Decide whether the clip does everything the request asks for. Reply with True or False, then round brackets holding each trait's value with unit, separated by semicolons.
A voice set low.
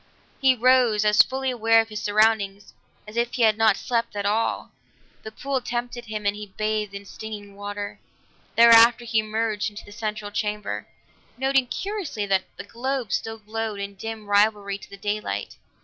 False (215 Hz)